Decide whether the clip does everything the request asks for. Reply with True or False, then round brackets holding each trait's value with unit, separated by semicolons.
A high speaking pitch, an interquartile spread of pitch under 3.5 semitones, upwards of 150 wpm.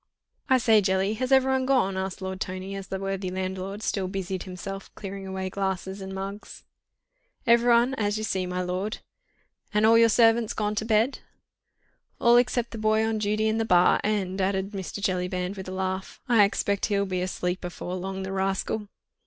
True (195 Hz; 2.5 semitones; 185 wpm)